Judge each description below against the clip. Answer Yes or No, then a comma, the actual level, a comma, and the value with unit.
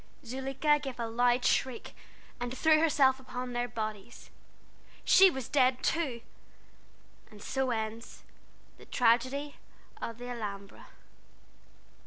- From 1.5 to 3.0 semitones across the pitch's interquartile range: Yes, narrow, 2.5 semitones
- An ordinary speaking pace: No, slow, 115 wpm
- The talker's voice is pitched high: Yes, very high, 250 Hz